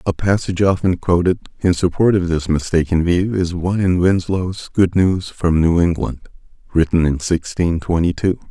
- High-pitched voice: No, very low, 90 Hz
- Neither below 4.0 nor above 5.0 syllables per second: Yes, 4.9 syllables/s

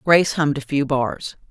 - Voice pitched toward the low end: No, medium, 145 Hz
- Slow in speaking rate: No, average, 200 wpm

